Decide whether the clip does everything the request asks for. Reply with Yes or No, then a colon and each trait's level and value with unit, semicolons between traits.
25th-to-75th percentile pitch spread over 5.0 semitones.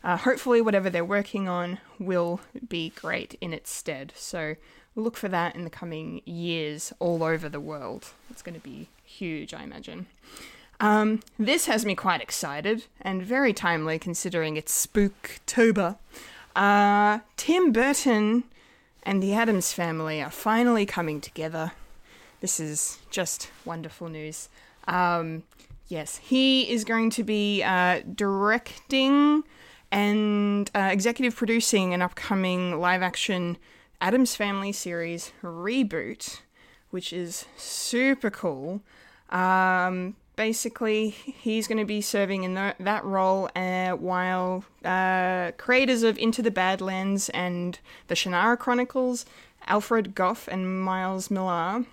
No: average, 4.2 semitones